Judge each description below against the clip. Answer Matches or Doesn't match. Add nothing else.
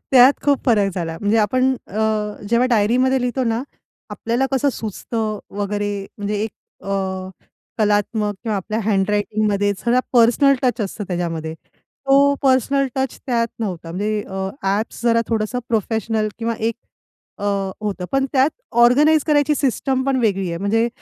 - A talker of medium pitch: Doesn't match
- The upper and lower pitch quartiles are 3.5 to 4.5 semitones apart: Matches